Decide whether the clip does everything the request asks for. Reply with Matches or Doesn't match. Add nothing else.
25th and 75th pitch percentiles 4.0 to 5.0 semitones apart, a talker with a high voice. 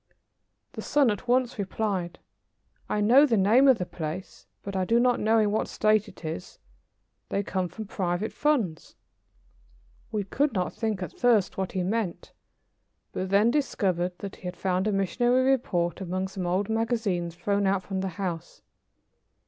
Doesn't match